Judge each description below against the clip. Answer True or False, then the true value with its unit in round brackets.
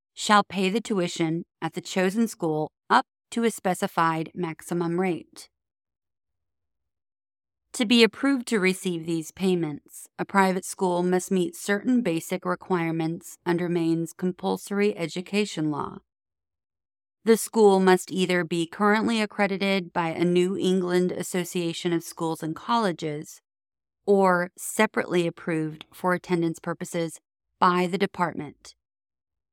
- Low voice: False (180 Hz)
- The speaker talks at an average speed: False (120 wpm)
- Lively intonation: False (2.9 semitones)